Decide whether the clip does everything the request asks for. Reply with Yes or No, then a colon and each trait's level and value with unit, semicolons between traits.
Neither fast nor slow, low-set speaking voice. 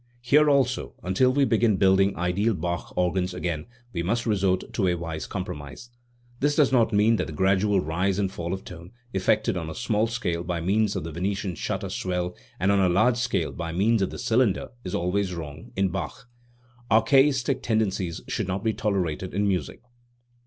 Yes: average, 190 wpm; very low, 95 Hz